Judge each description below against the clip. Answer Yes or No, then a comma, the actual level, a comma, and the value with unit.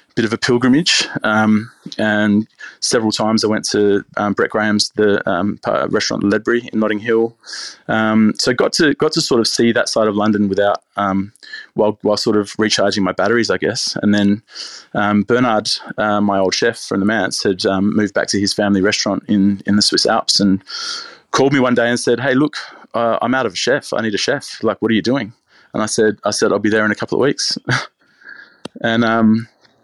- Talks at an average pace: No, fast, 220 wpm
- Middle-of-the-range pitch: No, low, 105 Hz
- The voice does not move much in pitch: Yes, narrow, 1.4 semitones